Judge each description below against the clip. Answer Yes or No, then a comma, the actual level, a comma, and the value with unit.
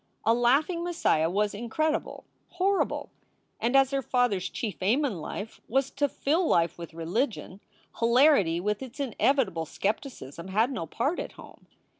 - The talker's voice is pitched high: Yes, high, 235 Hz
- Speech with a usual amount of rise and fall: No, wide, 6.5 semitones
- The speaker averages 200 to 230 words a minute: No, average, 160 wpm